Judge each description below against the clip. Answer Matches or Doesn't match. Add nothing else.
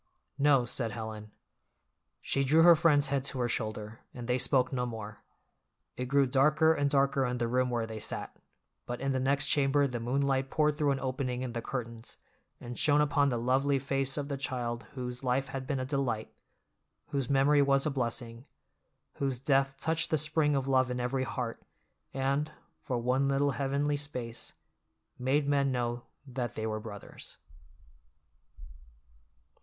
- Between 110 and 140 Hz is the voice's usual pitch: Matches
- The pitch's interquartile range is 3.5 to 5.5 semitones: Doesn't match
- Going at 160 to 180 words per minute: Matches